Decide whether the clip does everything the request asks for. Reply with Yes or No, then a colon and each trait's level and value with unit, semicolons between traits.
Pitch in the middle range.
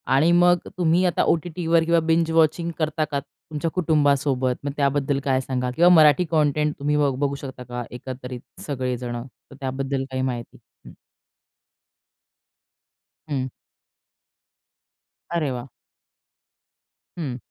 Yes: medium, 145 Hz